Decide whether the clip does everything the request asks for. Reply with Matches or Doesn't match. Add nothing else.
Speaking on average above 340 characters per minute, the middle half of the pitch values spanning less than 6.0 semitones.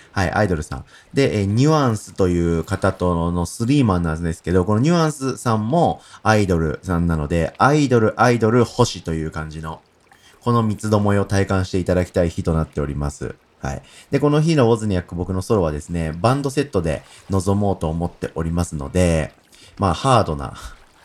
Matches